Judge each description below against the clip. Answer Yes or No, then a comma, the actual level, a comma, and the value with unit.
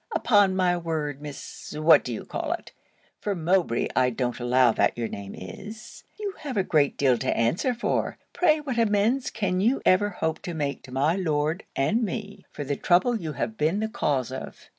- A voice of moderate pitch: Yes, medium, 175 Hz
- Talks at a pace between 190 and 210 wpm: Yes, average, 195 wpm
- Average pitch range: No, wide, 6.8 semitones